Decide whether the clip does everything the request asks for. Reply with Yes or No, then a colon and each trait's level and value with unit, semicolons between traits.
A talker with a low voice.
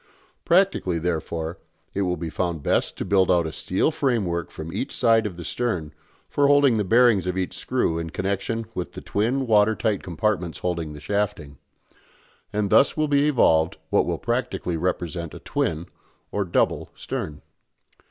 Yes: very low, 95 Hz